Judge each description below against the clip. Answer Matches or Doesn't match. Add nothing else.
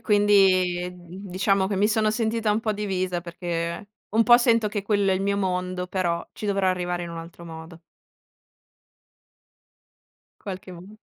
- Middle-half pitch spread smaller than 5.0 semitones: Matches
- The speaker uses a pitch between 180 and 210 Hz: Matches